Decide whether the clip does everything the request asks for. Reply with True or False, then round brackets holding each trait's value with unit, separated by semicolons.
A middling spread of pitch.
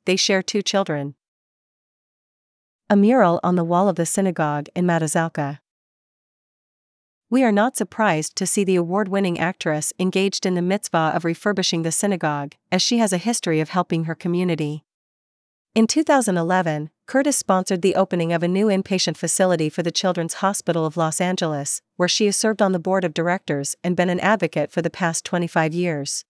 True (3.0 semitones)